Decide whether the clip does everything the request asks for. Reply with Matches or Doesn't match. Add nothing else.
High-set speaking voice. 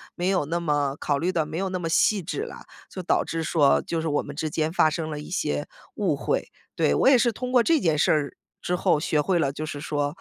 Doesn't match